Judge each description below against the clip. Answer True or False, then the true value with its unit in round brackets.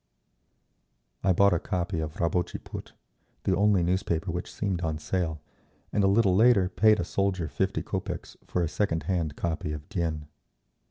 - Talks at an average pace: True (165 wpm)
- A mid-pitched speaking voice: False (90 Hz)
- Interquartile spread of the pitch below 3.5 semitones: True (3.1 semitones)